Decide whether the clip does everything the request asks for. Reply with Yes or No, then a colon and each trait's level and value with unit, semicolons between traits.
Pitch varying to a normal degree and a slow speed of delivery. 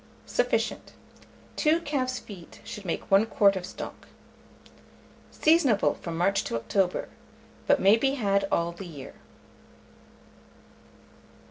No: wide, 6.2 semitones; slow, 115 wpm